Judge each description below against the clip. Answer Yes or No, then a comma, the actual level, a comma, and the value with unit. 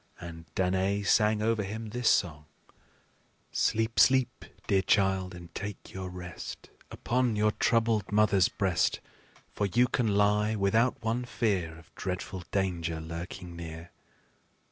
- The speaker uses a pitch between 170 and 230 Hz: No, low, 100 Hz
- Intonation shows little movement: No, average, 3.7 semitones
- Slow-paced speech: Yes, slow, 130 wpm